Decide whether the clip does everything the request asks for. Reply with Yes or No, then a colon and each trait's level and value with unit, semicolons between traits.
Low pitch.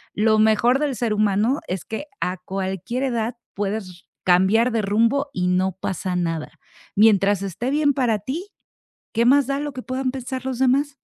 No: high, 225 Hz